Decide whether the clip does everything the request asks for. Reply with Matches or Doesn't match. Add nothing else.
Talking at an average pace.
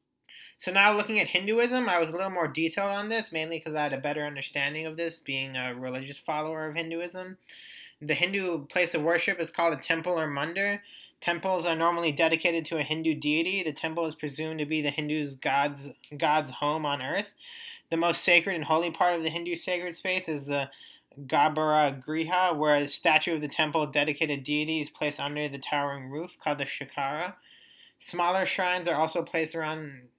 Matches